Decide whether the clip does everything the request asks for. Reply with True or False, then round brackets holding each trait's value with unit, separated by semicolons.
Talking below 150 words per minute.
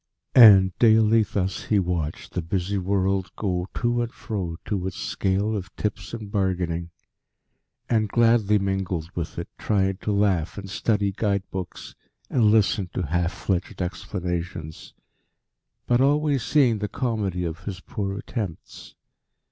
True (140 wpm)